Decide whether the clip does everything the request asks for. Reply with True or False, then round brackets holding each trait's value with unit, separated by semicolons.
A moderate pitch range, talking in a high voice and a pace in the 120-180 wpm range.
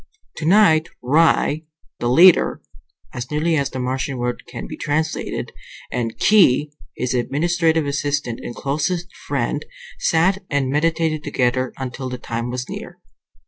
False (4.3 semitones; 145 Hz; 135 wpm)